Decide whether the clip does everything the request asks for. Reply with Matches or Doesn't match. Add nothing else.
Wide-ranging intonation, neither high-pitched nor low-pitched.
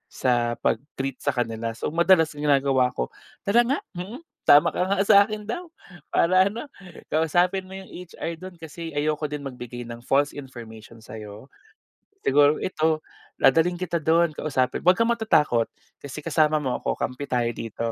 Matches